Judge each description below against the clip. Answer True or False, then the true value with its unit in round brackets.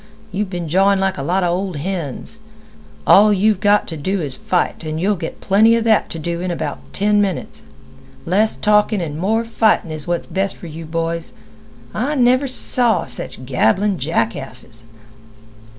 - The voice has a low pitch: False (185 Hz)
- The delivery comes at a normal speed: True (175 wpm)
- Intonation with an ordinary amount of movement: True (4.4 semitones)